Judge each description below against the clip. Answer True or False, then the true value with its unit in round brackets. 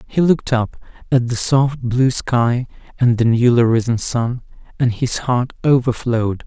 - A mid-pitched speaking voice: False (120 Hz)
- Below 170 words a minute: True (160 wpm)